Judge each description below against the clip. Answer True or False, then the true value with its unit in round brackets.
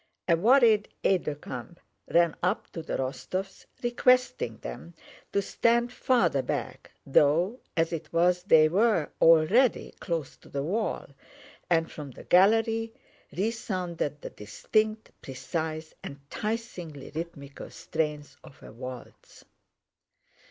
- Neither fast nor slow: False (120 wpm)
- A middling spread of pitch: False (6.3 semitones)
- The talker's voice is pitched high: False (170 Hz)